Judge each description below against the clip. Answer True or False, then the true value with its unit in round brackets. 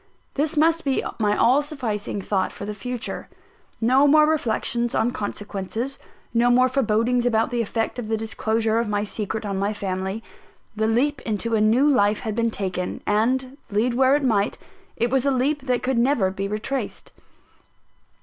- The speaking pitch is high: True (230 Hz)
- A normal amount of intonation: True (3.7 semitones)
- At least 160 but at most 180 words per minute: True (175 wpm)